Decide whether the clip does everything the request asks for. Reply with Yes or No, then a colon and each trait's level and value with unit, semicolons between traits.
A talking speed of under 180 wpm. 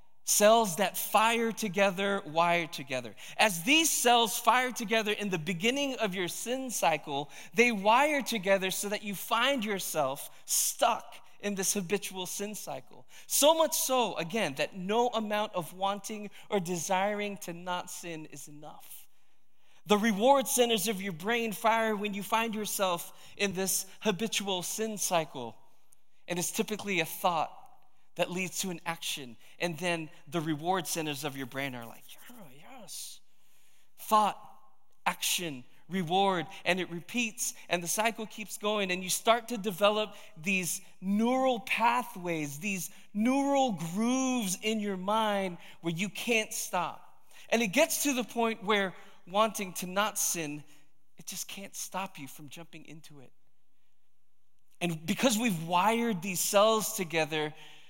Yes: average, 145 wpm